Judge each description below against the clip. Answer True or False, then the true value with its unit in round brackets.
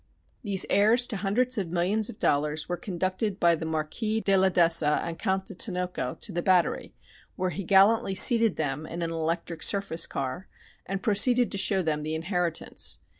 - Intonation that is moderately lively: True (3.5 semitones)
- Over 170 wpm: True (180 wpm)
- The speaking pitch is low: False (185 Hz)